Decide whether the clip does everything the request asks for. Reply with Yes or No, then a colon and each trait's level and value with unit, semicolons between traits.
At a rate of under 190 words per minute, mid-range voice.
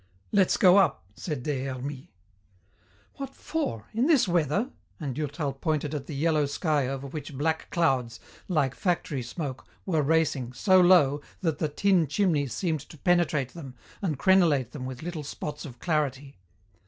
Yes: average, 160 wpm; medium, 150 Hz